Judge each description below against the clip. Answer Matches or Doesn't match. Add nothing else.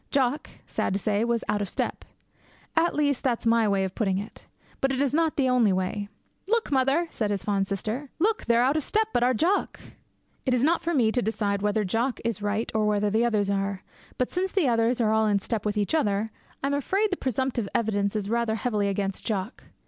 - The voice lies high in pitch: Matches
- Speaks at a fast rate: Matches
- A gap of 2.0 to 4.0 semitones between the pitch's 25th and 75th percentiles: Doesn't match